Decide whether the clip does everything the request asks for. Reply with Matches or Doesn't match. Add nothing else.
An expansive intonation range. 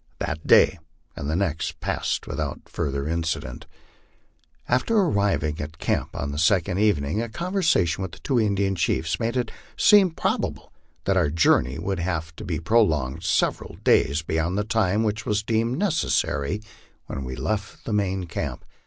Matches